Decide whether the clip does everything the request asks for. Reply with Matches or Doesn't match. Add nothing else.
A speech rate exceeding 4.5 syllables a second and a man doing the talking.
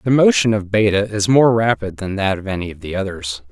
Matches